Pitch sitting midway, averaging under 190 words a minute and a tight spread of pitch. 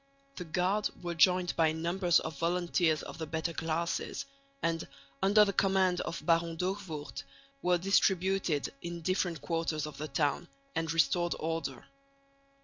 Yes: medium, 170 Hz; average, 140 wpm; narrow, 2.2 semitones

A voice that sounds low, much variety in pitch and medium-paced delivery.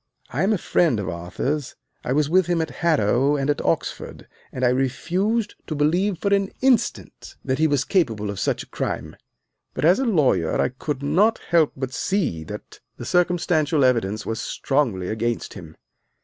No: medium, 145 Hz; wide, 6.3 semitones; average, 180 wpm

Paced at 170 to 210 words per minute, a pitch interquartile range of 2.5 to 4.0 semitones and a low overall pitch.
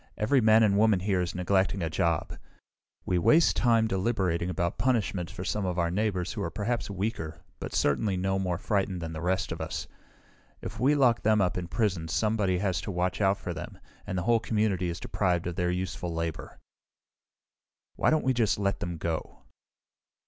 Yes: average, 190 wpm; average, 3.6 semitones; very low, 95 Hz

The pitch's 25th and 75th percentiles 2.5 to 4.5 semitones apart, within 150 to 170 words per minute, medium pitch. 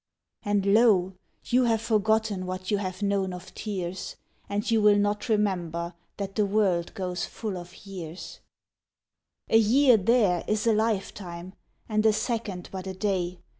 No: average, 2.8 semitones; average, 155 wpm; high, 200 Hz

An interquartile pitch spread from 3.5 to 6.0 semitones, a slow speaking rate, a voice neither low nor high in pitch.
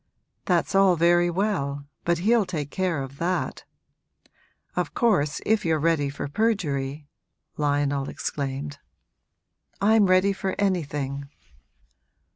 Yes: average, 5.2 semitones; slow, 115 wpm; medium, 165 Hz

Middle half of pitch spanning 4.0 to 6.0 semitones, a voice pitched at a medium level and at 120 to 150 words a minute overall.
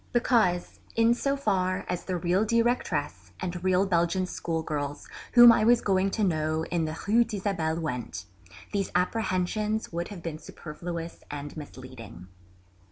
Yes: average, 5.0 semitones; medium, 180 Hz; average, 145 wpm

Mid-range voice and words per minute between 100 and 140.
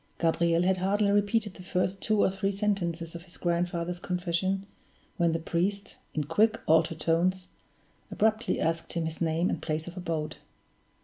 No: medium, 175 Hz; average, 165 wpm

